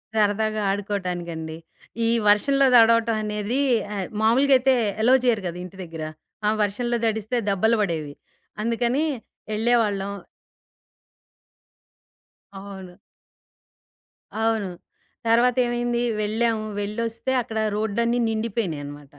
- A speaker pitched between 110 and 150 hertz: No, high, 220 Hz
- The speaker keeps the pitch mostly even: No, average, 3.2 semitones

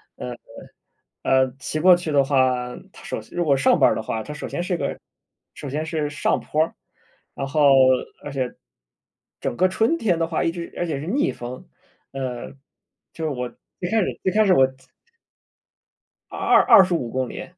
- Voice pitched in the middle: Yes, medium, 150 Hz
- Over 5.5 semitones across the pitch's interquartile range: No, average, 5.1 semitones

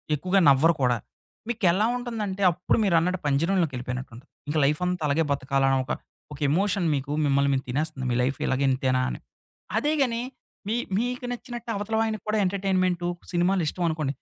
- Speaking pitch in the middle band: Yes, medium, 175 Hz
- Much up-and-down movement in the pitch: Yes, wide, 6.5 semitones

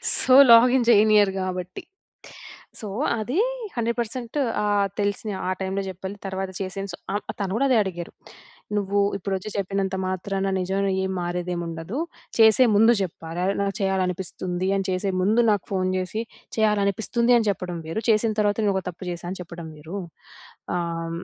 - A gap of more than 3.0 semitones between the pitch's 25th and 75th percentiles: No, narrow, 2.6 semitones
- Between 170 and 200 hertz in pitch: Yes, high, 195 Hz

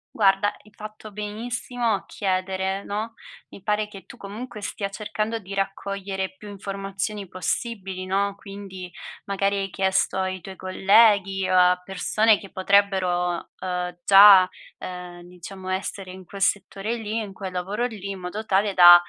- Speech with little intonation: Yes, narrow, 1.8 semitones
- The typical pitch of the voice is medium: No, high, 195 Hz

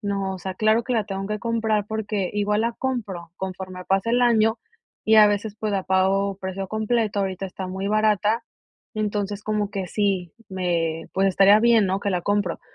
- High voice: Yes, high, 205 Hz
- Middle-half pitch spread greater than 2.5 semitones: No, narrow, 2.2 semitones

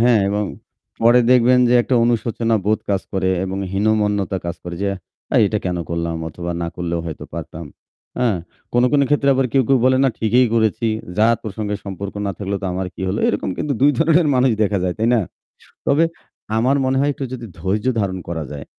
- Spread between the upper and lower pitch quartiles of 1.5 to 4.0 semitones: No, average, 4.7 semitones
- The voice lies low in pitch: Yes, low, 105 Hz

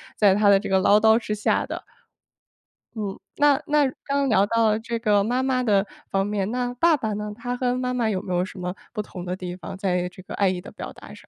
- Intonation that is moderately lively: Yes, average, 4.2 semitones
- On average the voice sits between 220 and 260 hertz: No, high, 210 Hz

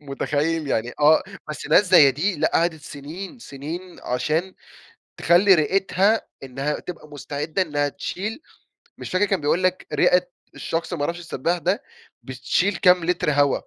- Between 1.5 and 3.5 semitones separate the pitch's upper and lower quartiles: No, average, 4.1 semitones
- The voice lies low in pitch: No, medium, 165 Hz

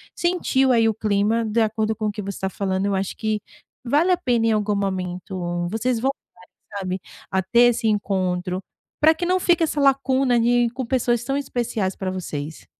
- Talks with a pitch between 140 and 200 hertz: No, high, 220 Hz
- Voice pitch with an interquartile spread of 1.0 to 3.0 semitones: No, average, 4.5 semitones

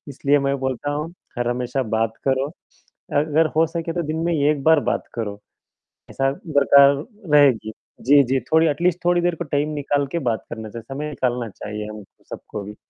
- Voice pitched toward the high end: No, medium, 140 Hz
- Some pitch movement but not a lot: Yes, average, 4.3 semitones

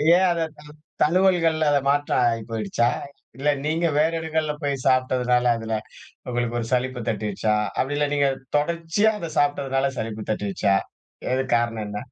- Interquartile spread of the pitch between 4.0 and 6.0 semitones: Yes, average, 4.9 semitones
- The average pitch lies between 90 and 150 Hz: Yes, low, 135 Hz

